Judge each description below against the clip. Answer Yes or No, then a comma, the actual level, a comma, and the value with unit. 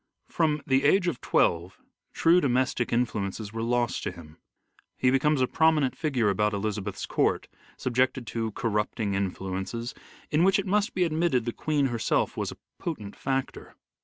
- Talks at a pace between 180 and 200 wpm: No, average, 160 wpm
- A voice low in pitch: Yes, low, 125 Hz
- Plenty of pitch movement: Yes, wide, 6.1 semitones